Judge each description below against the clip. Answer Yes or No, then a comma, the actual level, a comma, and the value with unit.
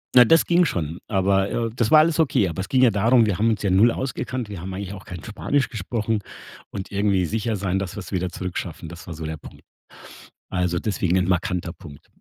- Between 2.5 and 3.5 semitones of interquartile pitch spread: No, average, 4.1 semitones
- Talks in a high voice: No, low, 100 Hz